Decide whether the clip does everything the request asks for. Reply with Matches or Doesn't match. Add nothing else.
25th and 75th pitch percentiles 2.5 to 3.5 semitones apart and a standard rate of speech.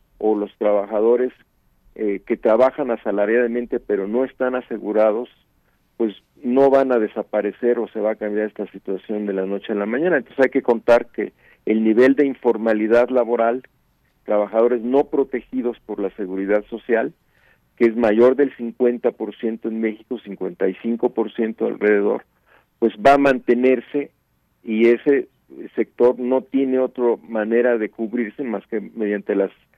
Matches